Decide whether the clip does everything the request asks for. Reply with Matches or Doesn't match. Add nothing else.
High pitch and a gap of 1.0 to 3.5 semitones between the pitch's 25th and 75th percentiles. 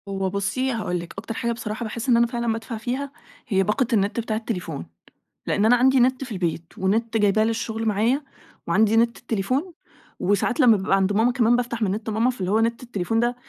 Matches